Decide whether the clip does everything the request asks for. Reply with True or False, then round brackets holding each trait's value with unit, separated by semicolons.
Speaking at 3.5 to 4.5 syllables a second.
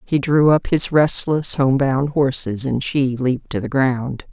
True (4.0 syllables/s)